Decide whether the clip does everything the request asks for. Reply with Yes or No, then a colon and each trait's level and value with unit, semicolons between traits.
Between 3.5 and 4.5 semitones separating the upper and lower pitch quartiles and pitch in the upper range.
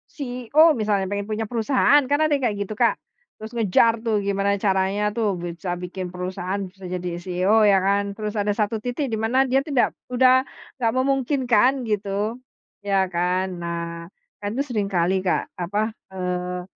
Yes: average, 4.1 semitones; high, 205 Hz